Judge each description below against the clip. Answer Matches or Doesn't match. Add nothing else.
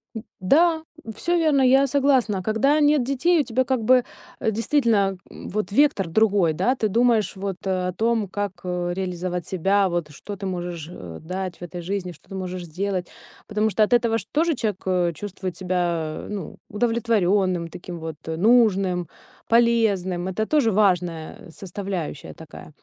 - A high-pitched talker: Matches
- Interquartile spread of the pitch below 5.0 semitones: Matches